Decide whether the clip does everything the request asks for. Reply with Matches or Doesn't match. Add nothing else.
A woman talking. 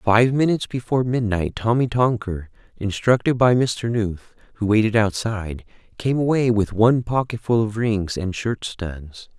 Doesn't match